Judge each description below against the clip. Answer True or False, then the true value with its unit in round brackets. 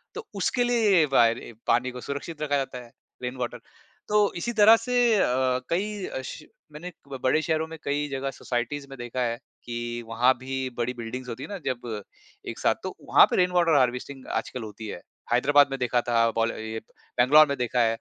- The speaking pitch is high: False (130 Hz)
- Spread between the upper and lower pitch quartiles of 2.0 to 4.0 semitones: False (4.6 semitones)